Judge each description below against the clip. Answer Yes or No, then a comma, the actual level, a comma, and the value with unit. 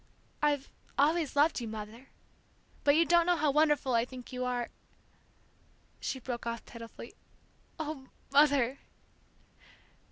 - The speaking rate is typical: No, slow, 130 wpm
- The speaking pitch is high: Yes, very high, 275 Hz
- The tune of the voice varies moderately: Yes, average, 3.8 semitones